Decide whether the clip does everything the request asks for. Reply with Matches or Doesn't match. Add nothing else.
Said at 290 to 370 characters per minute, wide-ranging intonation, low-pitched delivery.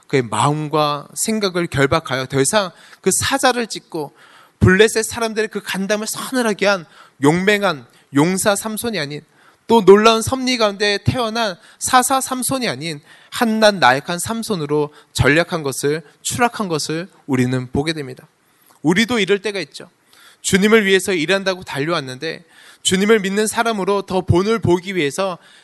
Doesn't match